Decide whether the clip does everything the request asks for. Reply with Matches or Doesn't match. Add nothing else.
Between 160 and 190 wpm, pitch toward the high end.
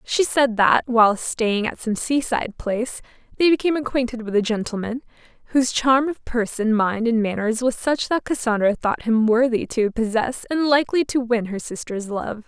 Matches